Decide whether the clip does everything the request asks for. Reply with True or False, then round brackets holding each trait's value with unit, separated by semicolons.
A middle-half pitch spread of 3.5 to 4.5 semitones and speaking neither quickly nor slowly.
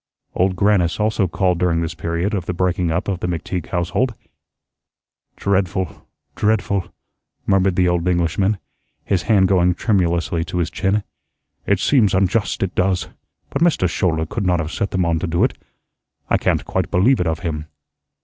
False (2.4 semitones; 170 wpm)